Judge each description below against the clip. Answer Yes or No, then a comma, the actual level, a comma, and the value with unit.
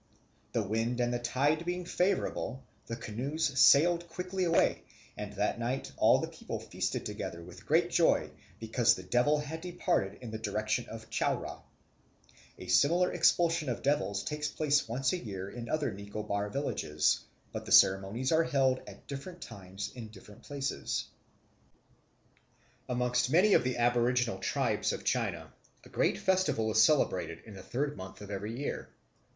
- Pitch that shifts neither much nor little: No, wide, 6.0 semitones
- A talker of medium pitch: No, low, 125 Hz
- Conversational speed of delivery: Yes, average, 160 wpm